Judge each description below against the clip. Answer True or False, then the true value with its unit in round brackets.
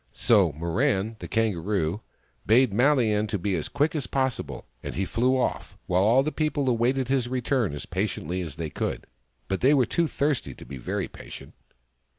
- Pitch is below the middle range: True (115 Hz)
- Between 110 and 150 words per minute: False (175 wpm)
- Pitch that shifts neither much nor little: False (6.1 semitones)